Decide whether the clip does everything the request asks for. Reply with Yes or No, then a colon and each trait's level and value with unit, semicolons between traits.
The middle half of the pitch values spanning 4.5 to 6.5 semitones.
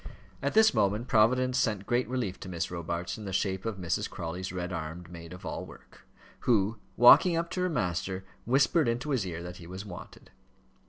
Yes: wide, 5.5 semitones